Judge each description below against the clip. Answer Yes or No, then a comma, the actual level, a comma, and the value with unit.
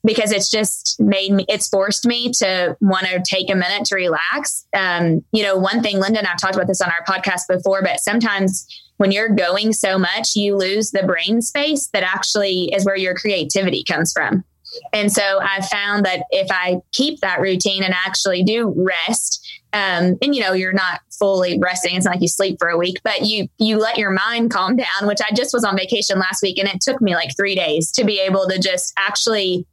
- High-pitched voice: Yes, high, 195 Hz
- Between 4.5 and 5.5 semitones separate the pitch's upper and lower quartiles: No, narrow, 2.4 semitones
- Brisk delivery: Yes, fast, 220 wpm